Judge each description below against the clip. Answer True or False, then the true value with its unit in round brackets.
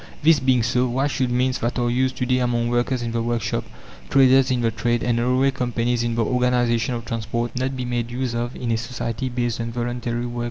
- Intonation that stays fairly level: True (1.3 semitones)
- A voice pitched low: True (120 Hz)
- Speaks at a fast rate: True (230 wpm)